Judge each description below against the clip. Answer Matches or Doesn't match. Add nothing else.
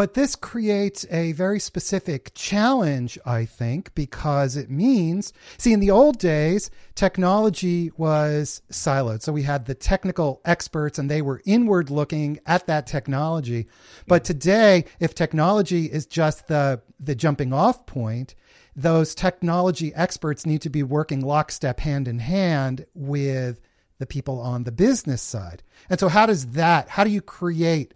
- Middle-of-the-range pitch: Matches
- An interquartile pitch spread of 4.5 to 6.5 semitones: Matches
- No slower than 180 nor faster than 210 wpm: Doesn't match